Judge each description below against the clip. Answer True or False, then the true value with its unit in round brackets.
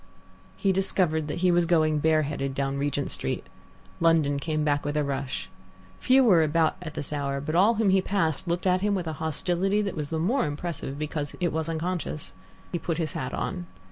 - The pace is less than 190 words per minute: False (205 wpm)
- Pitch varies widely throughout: False (3.5 semitones)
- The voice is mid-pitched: True (160 Hz)